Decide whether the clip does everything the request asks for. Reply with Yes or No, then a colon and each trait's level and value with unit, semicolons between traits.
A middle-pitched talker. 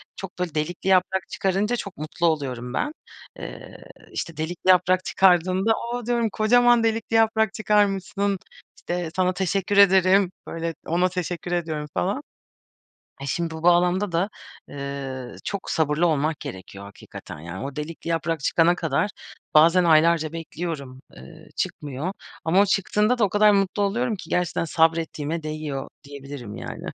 Yes: medium, 175 Hz